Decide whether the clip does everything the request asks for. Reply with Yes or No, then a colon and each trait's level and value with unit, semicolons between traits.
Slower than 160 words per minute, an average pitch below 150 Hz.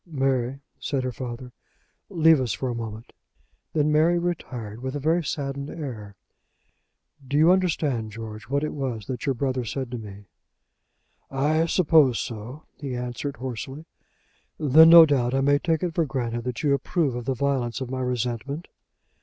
No: average, 170 wpm; low, 135 Hz